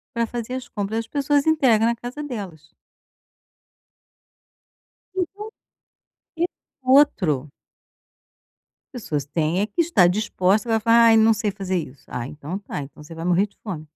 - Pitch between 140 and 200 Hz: No, high, 210 Hz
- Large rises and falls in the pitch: Yes, wide, 6.1 semitones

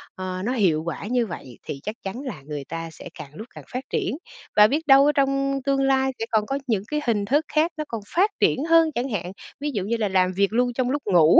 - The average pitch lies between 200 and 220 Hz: No, high, 235 Hz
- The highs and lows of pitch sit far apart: Yes, wide, 6.5 semitones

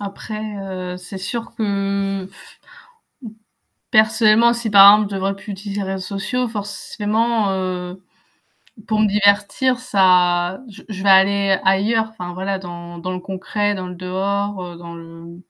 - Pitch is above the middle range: Yes, high, 195 Hz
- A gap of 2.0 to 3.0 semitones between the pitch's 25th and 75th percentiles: Yes, narrow, 2.4 semitones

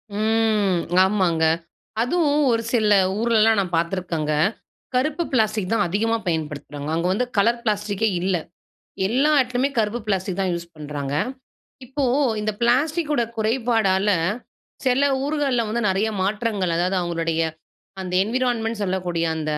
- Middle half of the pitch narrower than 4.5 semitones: No, average, 4.8 semitones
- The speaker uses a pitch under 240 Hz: Yes, high, 210 Hz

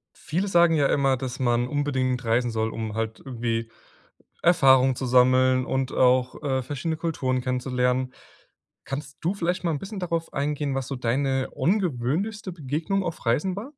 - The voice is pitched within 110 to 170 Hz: Yes, low, 135 Hz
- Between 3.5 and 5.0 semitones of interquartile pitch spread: Yes, average, 4.4 semitones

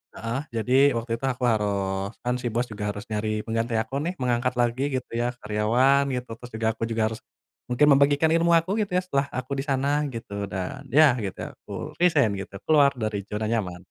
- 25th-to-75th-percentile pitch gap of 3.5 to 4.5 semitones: Yes, average, 4.1 semitones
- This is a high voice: No, low, 120 Hz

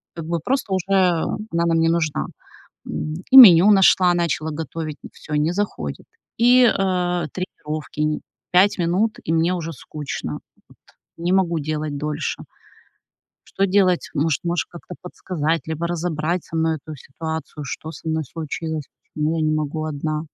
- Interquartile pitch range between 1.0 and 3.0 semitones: Yes, narrow, 2.6 semitones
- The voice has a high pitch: No, medium, 165 Hz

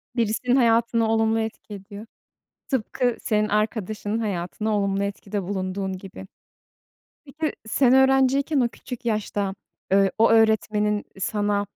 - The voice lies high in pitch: Yes, high, 215 Hz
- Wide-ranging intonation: No, narrow, 2.5 semitones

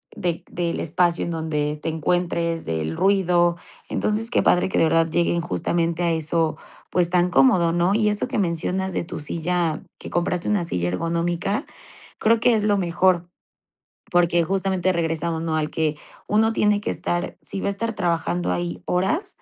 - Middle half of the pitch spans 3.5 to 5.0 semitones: No, narrow, 2.5 semitones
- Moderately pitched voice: Yes, medium, 175 Hz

